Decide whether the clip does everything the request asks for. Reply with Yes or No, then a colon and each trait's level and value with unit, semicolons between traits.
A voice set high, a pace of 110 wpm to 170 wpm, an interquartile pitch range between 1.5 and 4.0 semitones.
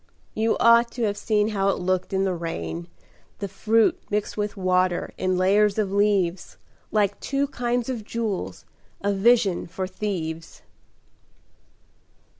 Yes: high, 200 Hz; average, 140 wpm; average, 2.9 semitones